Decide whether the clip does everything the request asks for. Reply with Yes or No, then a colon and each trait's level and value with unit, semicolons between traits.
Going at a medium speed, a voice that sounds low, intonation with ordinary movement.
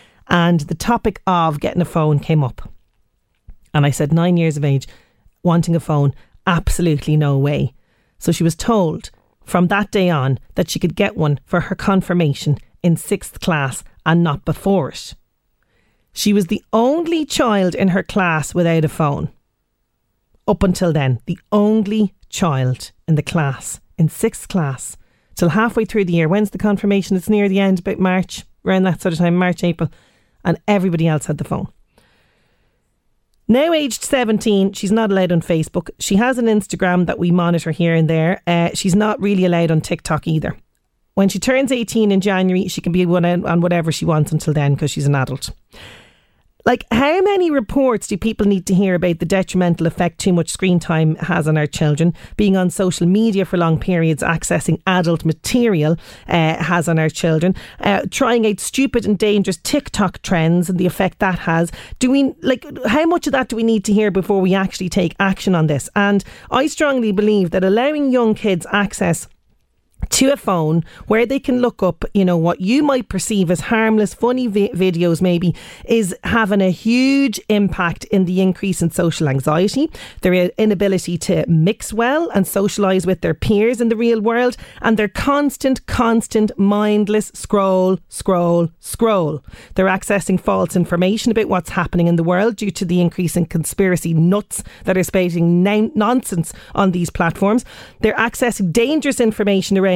No: average, 180 wpm; medium, 185 Hz; average, 4.0 semitones